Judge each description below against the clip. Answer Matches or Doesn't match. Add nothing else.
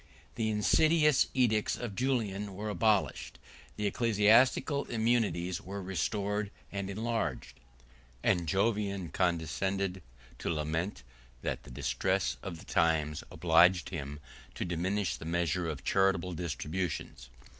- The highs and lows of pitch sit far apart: Doesn't match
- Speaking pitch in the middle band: Doesn't match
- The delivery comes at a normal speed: Doesn't match